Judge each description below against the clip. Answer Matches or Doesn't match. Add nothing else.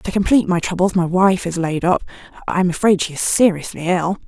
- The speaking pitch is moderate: Matches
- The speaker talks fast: Matches